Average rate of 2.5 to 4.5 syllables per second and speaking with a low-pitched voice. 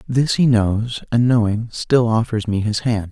Yes: 4.3 syllables/s; low, 115 Hz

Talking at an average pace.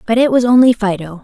No: fast, 245 wpm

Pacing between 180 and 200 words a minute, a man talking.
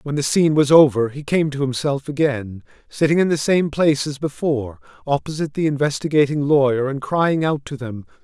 Yes: average, 190 wpm; male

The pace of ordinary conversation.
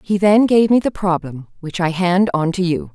No: fast, 245 wpm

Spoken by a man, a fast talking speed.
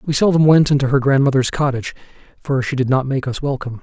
Yes: male; fast, 220 wpm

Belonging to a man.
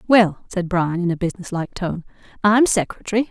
No: female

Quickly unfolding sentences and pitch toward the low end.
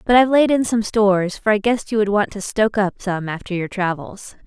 No: fast, 255 wpm; high, 205 Hz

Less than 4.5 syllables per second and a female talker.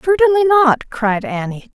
Yes: 4.2 syllables/s; female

